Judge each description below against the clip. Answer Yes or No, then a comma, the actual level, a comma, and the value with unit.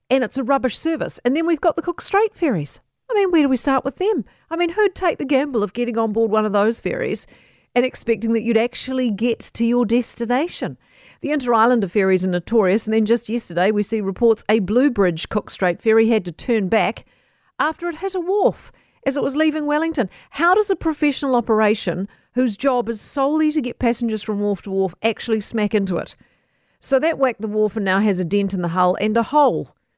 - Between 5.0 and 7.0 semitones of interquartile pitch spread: Yes, wide, 5.4 semitones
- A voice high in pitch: Yes, high, 235 Hz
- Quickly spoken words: Yes, fast, 220 wpm